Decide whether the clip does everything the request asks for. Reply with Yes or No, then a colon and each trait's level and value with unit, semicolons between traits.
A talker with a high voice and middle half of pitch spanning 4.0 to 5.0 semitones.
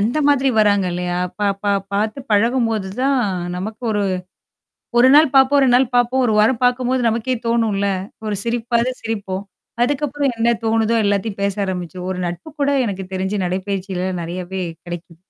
Yes: high, 215 Hz; average, 4.5 semitones